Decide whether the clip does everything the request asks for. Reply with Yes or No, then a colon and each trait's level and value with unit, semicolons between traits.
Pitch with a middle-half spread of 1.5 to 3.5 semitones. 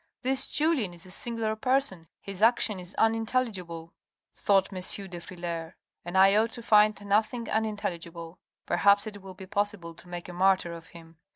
No: average, 3.9 semitones